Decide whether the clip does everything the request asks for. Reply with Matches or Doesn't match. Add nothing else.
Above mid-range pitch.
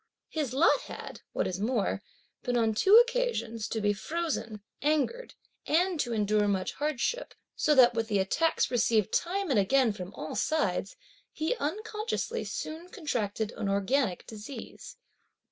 Matches